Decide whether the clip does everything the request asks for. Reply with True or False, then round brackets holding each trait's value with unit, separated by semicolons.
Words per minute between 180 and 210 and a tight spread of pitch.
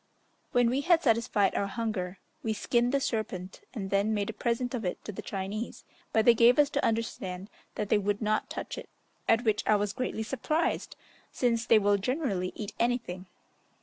False (190 wpm; 3.2 semitones)